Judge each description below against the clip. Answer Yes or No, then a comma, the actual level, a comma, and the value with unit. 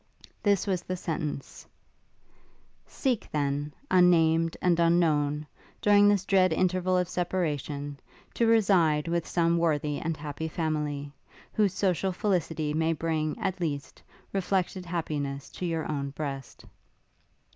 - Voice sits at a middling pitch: Yes, medium, 165 Hz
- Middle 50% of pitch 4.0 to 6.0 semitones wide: No, average, 3.5 semitones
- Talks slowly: Yes, slow, 125 wpm